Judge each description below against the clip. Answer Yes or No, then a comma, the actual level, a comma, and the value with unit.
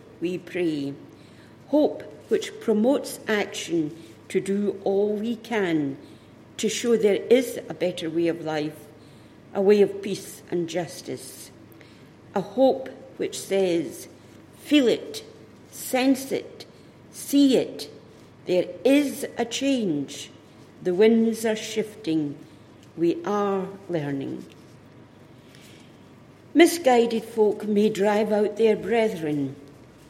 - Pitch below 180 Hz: No, high, 200 Hz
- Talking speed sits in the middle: No, slow, 110 wpm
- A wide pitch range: Yes, wide, 5.9 semitones